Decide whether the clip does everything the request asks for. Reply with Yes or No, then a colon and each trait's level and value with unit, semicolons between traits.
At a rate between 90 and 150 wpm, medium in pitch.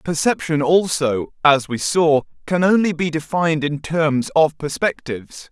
Yes: average, 140 wpm; medium, 155 Hz